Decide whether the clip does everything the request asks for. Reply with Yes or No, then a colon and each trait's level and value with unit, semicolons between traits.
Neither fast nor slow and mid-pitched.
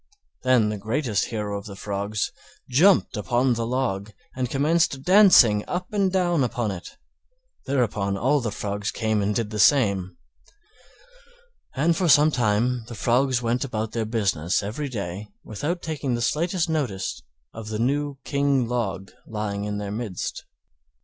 No: average, 150 wpm; low, 115 Hz